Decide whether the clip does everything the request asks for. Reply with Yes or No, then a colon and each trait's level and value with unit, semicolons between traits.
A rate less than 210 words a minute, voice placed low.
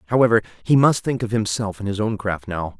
No: fast, 235 wpm; low, 110 Hz